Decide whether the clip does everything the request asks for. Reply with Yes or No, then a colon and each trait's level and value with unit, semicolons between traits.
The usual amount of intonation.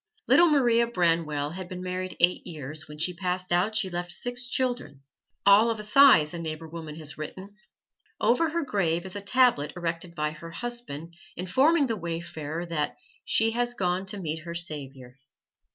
No: wide, 5.7 semitones